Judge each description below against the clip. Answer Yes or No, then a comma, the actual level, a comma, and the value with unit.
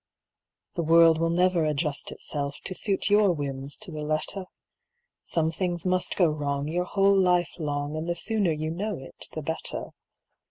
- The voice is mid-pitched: Yes, medium, 165 Hz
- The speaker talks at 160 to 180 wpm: Yes, average, 170 wpm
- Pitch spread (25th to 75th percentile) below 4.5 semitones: Yes, average, 3.3 semitones